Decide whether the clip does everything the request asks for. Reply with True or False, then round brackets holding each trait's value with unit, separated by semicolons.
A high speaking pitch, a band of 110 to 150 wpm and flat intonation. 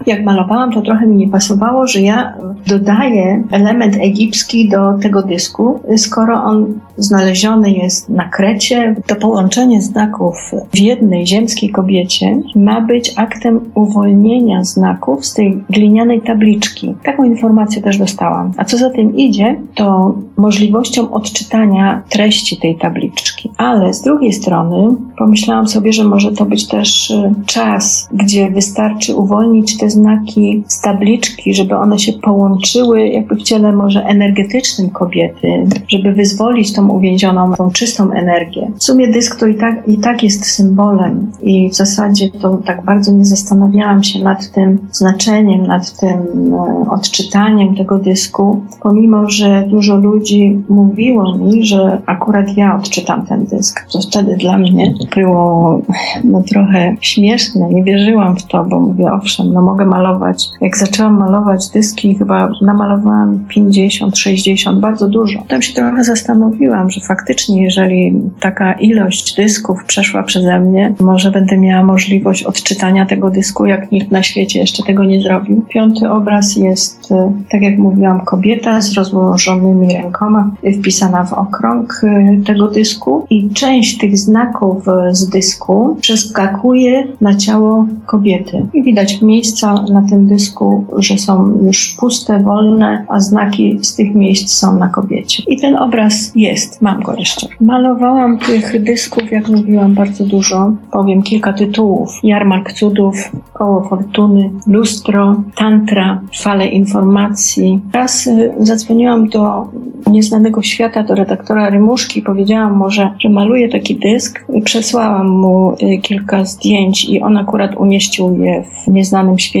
True (205 Hz; 140 wpm; 2.1 semitones)